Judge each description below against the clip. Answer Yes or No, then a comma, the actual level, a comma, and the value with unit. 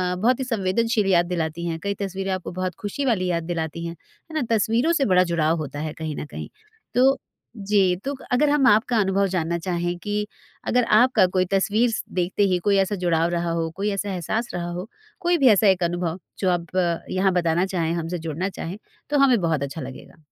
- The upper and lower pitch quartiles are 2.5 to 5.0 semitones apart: Yes, average, 3.7 semitones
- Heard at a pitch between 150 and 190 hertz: Yes, medium, 185 Hz